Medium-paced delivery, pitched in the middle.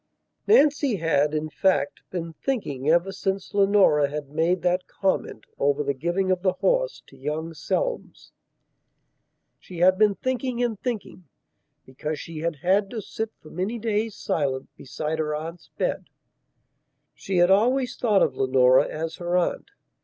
Yes: average, 155 wpm; medium, 180 Hz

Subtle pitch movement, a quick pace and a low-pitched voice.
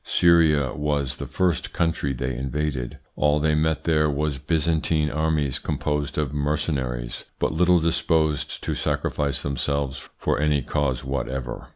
No: narrow, 2.3 semitones; average, 140 wpm; very low, 75 Hz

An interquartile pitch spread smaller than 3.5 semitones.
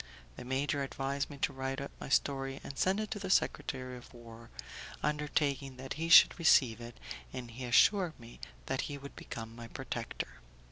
Yes: average, 3.0 semitones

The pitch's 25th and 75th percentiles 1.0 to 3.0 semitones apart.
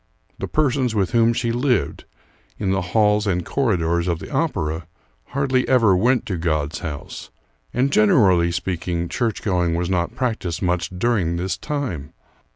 No: wide, 5.6 semitones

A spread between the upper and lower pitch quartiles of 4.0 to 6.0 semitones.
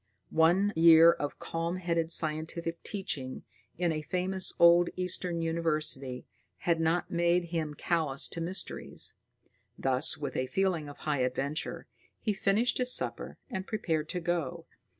No: narrow, 2.6 semitones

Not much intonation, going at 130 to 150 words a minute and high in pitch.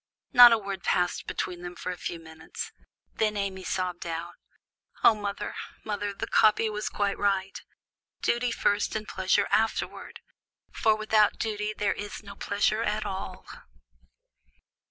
Yes: narrow, 2.2 semitones; average, 145 wpm; high, 205 Hz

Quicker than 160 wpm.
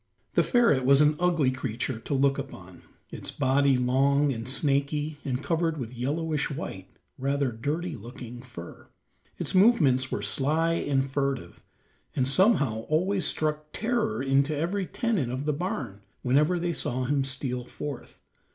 No: average, 150 wpm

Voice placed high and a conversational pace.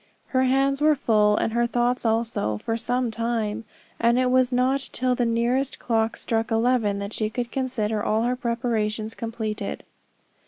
Yes: high, 235 Hz; average, 165 wpm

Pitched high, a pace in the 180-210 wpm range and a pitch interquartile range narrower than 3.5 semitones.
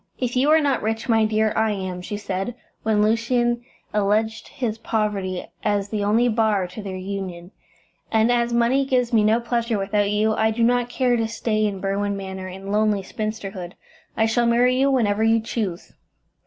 Yes: high, 220 Hz; average, 185 wpm; average, 2.8 semitones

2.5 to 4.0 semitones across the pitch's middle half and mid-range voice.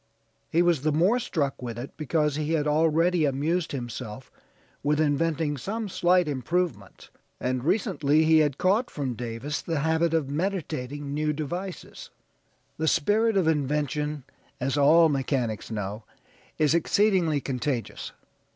Yes: average, 3.6 semitones; medium, 150 Hz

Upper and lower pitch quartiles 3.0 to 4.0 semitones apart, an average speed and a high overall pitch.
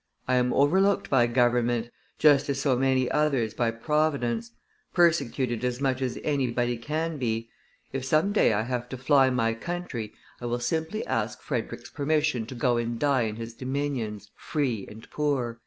No: average, 3.6 semitones; average, 170 wpm; low, 125 Hz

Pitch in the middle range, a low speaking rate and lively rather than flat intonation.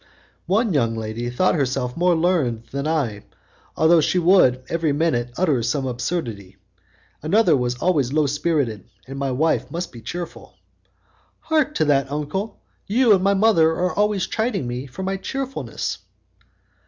No: medium, 155 Hz; average, 155 wpm; wide, 6.6 semitones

